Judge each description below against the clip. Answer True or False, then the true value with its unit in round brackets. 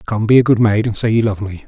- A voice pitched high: False (110 Hz)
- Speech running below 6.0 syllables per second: False (6.6 syllables/s)